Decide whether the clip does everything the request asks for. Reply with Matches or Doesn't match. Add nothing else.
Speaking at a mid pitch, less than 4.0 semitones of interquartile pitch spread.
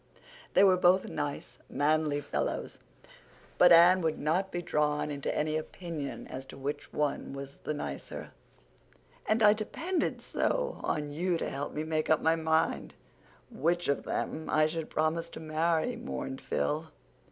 Matches